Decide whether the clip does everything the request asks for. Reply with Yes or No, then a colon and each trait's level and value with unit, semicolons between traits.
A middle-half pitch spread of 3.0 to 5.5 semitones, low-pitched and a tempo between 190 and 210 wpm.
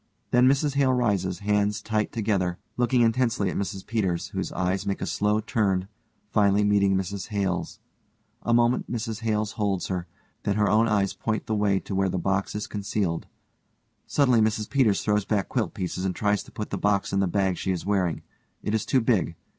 No: narrow, 2.4 semitones; low, 105 Hz; average, 195 wpm